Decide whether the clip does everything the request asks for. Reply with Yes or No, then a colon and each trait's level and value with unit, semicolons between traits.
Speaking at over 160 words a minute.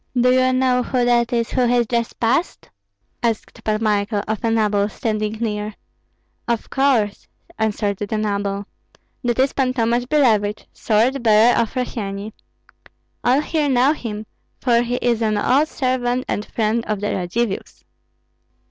No: average, 155 wpm